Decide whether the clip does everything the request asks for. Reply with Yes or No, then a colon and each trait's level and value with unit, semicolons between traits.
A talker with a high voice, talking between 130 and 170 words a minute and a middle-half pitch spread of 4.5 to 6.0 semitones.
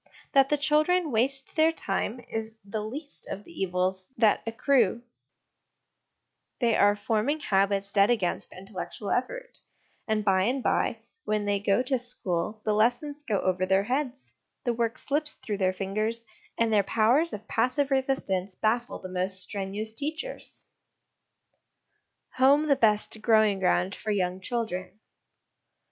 Yes: high, 220 Hz; average, 145 wpm; average, 5.0 semitones